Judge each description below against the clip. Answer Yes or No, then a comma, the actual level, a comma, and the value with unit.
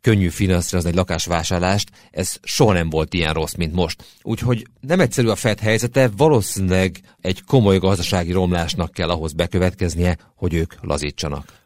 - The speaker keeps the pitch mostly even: No, average, 3.9 semitones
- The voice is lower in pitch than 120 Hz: Yes, very low, 90 Hz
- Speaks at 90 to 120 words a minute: No, average, 150 wpm